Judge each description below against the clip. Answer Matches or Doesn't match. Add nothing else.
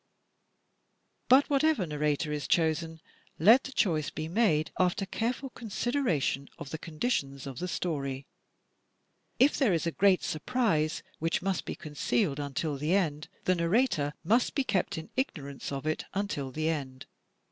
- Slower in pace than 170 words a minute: Matches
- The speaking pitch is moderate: Matches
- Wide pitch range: Matches